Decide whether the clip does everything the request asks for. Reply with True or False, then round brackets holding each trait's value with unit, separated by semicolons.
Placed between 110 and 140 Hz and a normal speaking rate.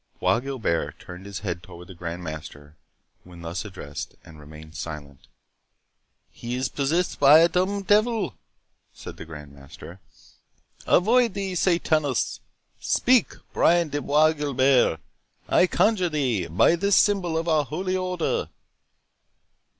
False (135 Hz; 130 wpm)